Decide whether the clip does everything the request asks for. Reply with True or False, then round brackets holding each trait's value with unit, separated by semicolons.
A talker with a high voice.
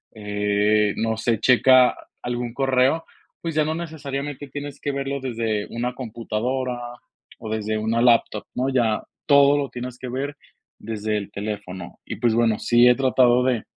False (120 Hz)